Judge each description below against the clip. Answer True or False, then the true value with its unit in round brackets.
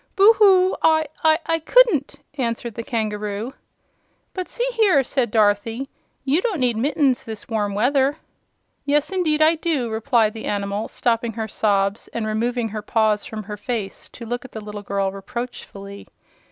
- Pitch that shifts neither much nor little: False (5.7 semitones)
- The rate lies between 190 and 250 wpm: False (165 wpm)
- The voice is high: True (235 Hz)